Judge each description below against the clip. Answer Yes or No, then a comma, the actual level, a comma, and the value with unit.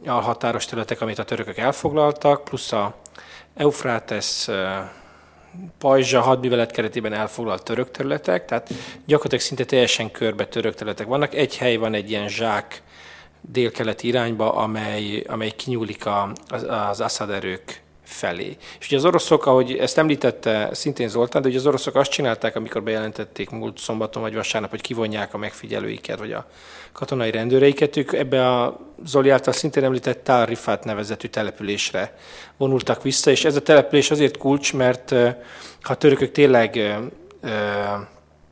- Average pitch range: Yes, average, 3.8 semitones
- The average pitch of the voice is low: Yes, low, 120 Hz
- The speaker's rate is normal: Yes, average, 140 wpm